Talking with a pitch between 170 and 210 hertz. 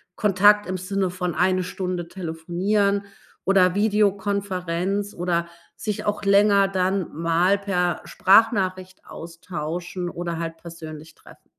Yes: medium, 185 Hz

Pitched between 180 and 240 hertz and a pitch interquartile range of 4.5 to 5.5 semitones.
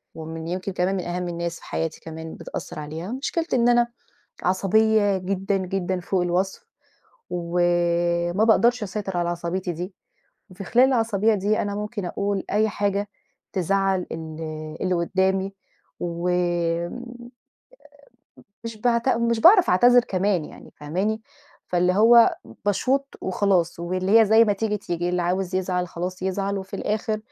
No: high, 190 Hz; average, 3.3 semitones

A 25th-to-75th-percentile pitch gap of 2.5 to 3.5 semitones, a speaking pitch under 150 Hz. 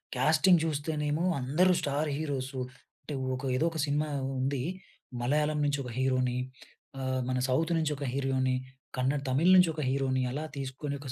Yes: average, 2.8 semitones; medium, 140 Hz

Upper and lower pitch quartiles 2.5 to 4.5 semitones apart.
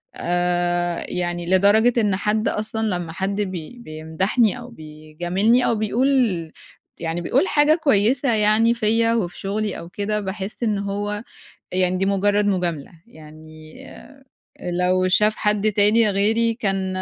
Yes: average, 3.7 semitones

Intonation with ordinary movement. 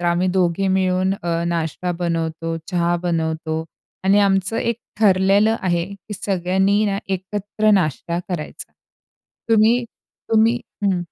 Yes: average, 3.0 semitones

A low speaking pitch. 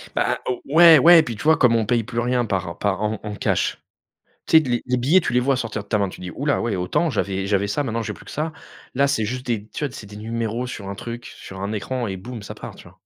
Yes: low, 115 Hz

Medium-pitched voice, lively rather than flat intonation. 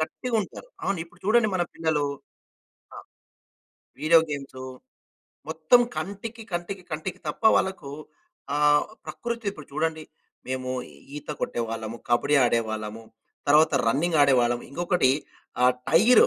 Yes: medium, 155 Hz; wide, 6.2 semitones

